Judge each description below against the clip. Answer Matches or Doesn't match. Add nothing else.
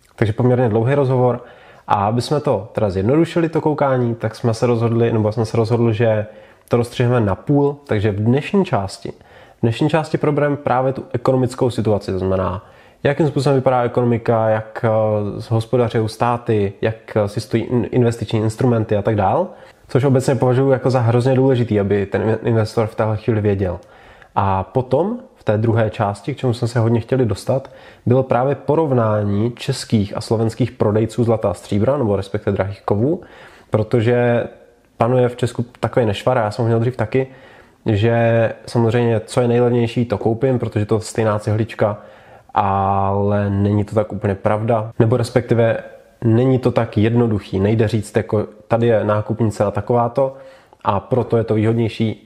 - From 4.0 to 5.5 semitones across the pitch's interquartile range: Doesn't match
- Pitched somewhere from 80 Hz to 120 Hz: Matches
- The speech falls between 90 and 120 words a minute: Doesn't match